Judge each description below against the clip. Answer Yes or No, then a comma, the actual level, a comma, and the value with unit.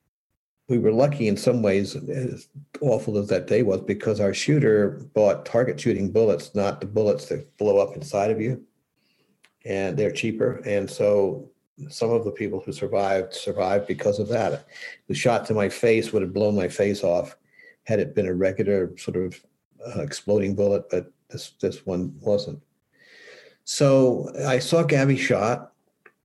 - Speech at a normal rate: Yes, average, 170 wpm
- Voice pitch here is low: Yes, low, 120 Hz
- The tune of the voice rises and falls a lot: Yes, wide, 6.2 semitones